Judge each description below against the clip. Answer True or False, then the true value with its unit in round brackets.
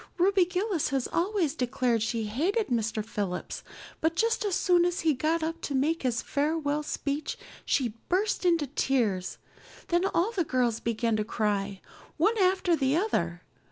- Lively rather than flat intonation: True (7.2 semitones)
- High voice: True (295 Hz)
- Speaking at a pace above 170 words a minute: False (160 wpm)